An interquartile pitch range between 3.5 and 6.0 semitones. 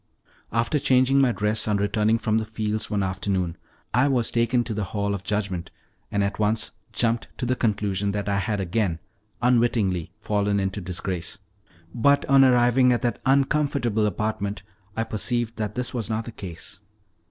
No: average, 3.0 semitones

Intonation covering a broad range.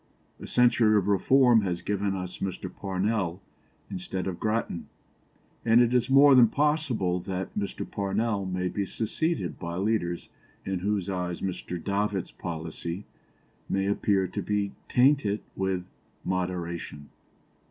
No: average, 3.4 semitones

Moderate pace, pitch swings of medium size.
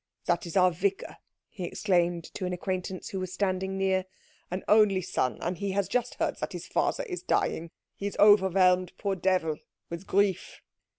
No: average, 180 wpm; narrow, 1.8 semitones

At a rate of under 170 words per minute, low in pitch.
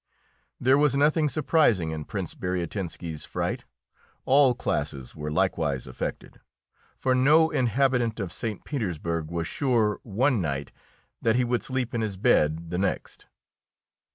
Yes: slow, 135 wpm; low, 110 Hz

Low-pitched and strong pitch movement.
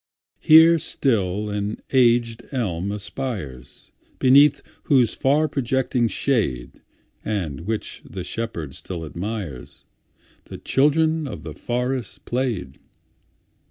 Yes: low, 115 Hz; wide, 5.7 semitones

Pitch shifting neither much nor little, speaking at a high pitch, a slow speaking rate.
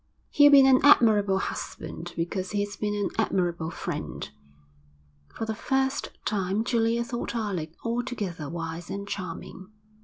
Yes: average, 4.8 semitones; high, 205 Hz; slow, 130 wpm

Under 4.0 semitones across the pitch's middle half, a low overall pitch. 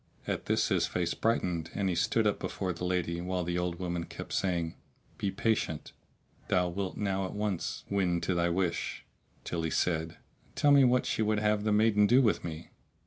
Yes: average, 3.3 semitones; very low, 90 Hz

